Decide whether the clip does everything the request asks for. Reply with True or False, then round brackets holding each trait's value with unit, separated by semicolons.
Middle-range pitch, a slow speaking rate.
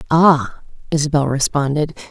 True (150 Hz; 85 wpm)